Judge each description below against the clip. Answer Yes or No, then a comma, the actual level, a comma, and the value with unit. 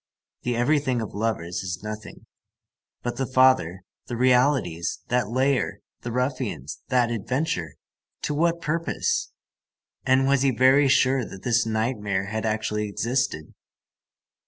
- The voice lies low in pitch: Yes, low, 120 Hz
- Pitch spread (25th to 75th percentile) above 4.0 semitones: No, average, 3.7 semitones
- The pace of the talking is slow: Yes, slow, 130 wpm